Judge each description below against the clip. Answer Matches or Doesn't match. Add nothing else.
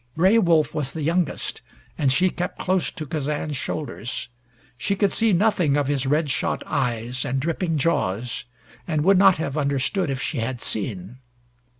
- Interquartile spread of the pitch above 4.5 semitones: Matches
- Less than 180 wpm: Matches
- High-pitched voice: Doesn't match